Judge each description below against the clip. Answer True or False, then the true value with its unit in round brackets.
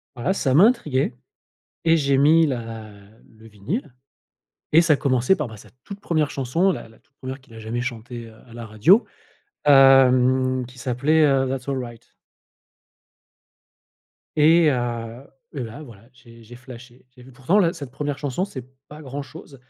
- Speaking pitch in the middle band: False (130 Hz)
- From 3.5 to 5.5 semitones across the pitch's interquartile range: True (3.8 semitones)